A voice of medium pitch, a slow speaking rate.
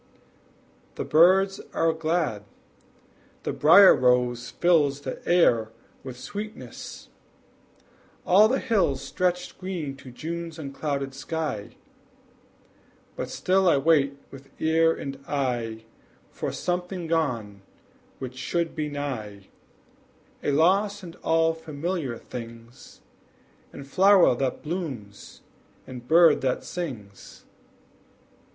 Yes: medium, 150 Hz; slow, 105 wpm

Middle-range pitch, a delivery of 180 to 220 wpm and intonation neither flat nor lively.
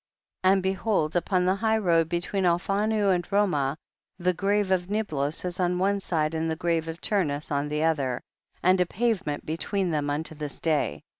Yes: medium, 175 Hz; average, 190 wpm; average, 3.8 semitones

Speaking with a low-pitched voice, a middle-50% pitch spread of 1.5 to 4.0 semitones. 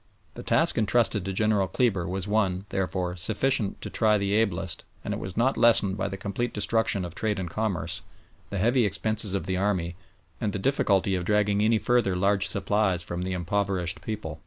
Yes: low, 100 Hz; average, 2.7 semitones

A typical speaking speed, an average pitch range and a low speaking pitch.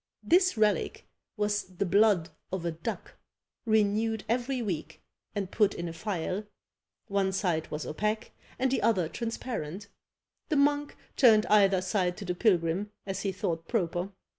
No: average, 150 wpm; average, 3.8 semitones; high, 200 Hz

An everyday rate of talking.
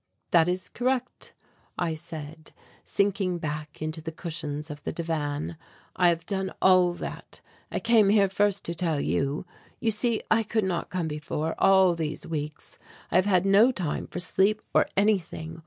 Yes: average, 170 wpm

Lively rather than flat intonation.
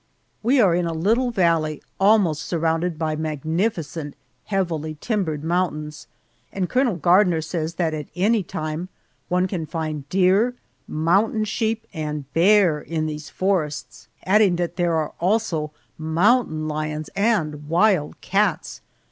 No: average, 4.1 semitones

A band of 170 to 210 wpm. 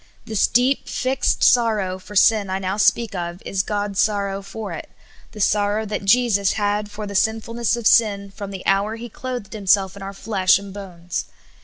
Yes: average, 190 wpm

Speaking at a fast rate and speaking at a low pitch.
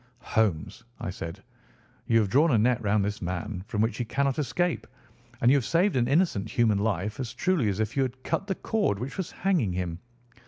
Yes: fast, 210 wpm; low, 115 Hz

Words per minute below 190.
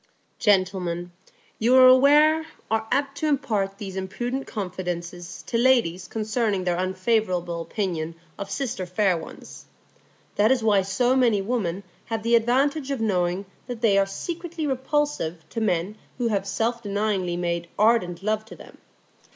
Yes: average, 150 wpm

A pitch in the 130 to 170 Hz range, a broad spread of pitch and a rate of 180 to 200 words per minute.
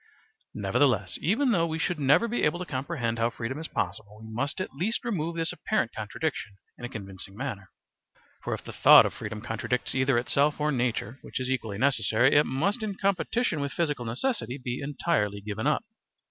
Yes: low, 135 Hz; wide, 6.4 semitones; average, 190 wpm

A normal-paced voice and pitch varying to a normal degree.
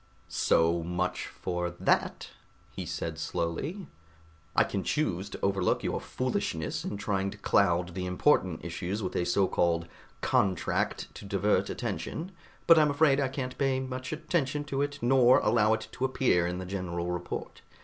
No: average, 160 wpm; wide, 7.0 semitones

